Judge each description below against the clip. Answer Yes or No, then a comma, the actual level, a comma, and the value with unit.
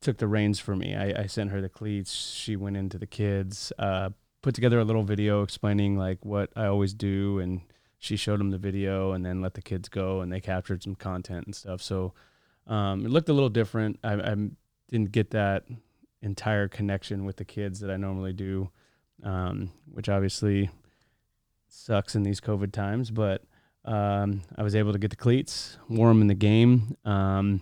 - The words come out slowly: No, average, 195 wpm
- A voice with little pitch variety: Yes, narrow, 1.8 semitones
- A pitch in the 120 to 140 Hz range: No, low, 100 Hz